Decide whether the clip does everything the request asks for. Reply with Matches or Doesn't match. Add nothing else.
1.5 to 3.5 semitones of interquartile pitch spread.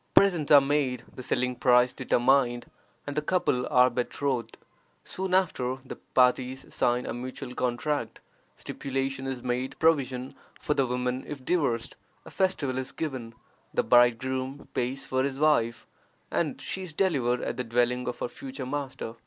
Matches